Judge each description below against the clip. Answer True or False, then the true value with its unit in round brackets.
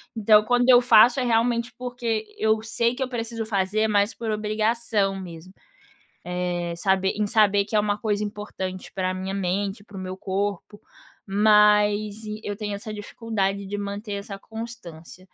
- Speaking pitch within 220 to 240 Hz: False (210 Hz)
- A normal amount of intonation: False (2.3 semitones)